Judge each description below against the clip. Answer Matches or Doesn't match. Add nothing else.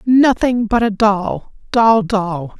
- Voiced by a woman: Matches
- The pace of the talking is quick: Doesn't match